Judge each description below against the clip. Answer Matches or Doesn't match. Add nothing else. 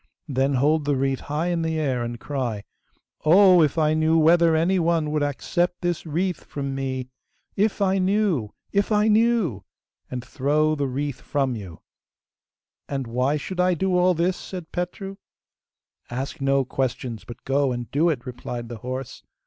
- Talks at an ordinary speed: Matches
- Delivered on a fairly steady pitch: Doesn't match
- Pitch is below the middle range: Doesn't match